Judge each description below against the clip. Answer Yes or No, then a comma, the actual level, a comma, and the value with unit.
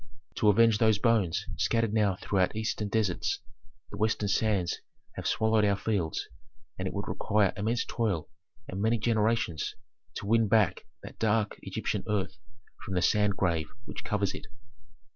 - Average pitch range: No, narrow, 2.3 semitones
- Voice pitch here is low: Yes, low, 105 Hz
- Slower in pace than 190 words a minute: Yes, average, 155 wpm